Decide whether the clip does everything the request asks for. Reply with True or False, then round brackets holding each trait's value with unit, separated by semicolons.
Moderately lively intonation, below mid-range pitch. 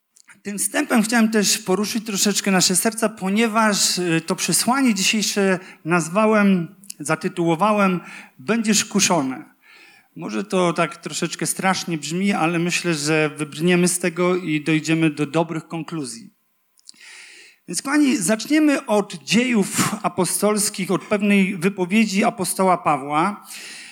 False (3.8 semitones; 190 Hz)